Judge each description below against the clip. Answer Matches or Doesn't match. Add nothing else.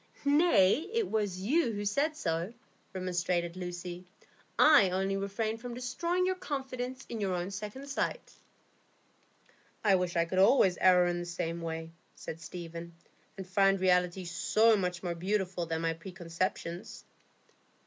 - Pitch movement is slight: Doesn't match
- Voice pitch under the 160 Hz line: Doesn't match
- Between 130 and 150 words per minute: Matches